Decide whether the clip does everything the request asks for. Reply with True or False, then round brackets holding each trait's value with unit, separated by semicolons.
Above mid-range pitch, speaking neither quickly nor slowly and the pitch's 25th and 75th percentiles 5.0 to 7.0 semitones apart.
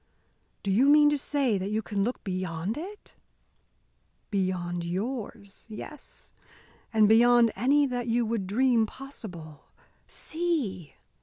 False (220 Hz; 125 wpm; 5.6 semitones)